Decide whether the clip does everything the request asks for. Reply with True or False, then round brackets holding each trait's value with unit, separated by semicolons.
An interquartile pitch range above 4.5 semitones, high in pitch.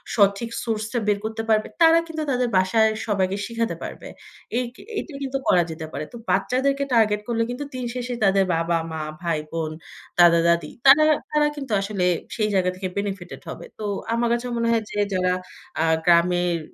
True (5.1 semitones; 210 Hz)